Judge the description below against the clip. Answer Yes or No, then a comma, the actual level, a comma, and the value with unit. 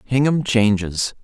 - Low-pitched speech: Yes, low, 115 Hz